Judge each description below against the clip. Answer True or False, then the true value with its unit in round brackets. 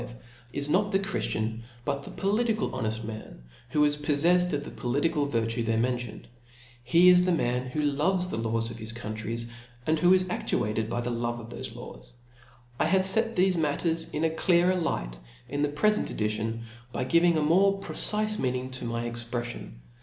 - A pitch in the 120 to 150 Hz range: True (140 Hz)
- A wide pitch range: True (6.9 semitones)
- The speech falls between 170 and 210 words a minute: True (175 wpm)